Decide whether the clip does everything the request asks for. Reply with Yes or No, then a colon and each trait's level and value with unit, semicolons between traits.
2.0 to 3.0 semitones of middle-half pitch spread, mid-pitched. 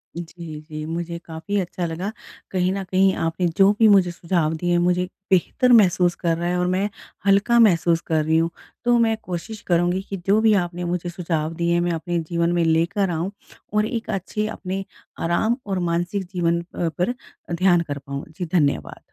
Yes: narrow, 2.4 semitones; medium, 175 Hz